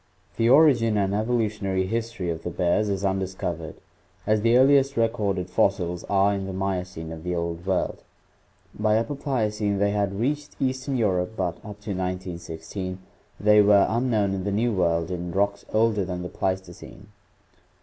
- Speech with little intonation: No, average, 3.4 semitones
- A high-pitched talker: No, low, 100 Hz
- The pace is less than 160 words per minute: No, average, 165 wpm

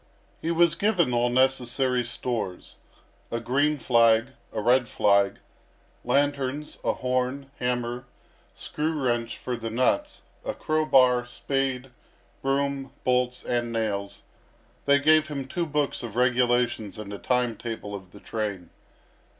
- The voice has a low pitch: Yes, low, 125 Hz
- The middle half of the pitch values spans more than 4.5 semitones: No, average, 3.1 semitones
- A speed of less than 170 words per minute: Yes, slow, 135 wpm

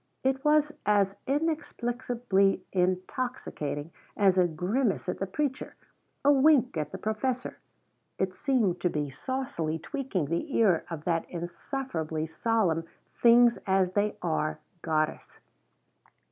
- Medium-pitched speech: No, high, 195 Hz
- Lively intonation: Yes, wide, 7.4 semitones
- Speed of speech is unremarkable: No, slow, 120 wpm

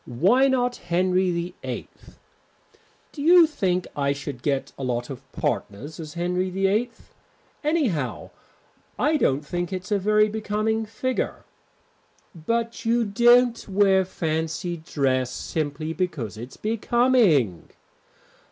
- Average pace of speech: No, slow, 115 wpm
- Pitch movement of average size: No, wide, 7.4 semitones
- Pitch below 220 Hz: Yes, medium, 185 Hz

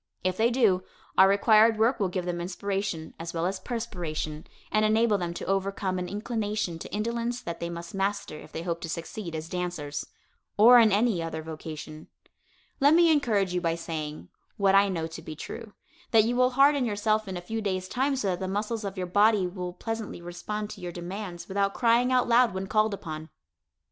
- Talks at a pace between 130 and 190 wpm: No, fast, 205 wpm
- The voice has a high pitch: Yes, high, 195 Hz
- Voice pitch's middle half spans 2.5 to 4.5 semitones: Yes, average, 4.2 semitones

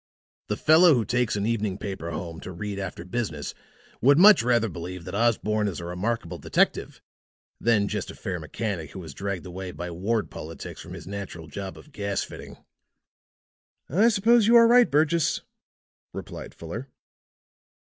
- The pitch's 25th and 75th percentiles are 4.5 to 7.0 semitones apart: Yes, wide, 5.4 semitones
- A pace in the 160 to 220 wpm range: Yes, average, 165 wpm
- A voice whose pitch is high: No, low, 100 Hz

